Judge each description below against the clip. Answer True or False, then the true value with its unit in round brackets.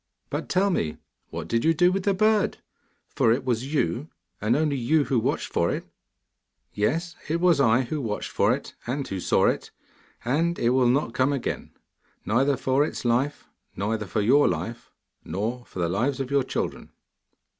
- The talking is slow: False (185 wpm)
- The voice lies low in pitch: True (130 Hz)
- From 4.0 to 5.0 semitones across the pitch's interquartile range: True (4.7 semitones)